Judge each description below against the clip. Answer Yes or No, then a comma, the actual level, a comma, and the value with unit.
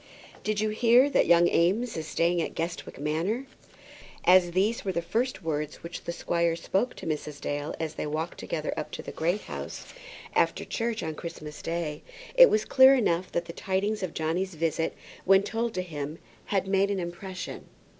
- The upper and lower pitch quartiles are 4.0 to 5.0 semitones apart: Yes, average, 4.3 semitones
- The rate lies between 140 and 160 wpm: No, average, 185 wpm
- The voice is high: No, medium, 175 Hz